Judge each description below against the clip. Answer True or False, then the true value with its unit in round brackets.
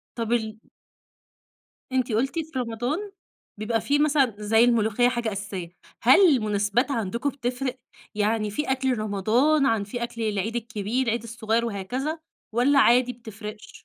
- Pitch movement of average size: True (3.1 semitones)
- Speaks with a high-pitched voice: True (235 Hz)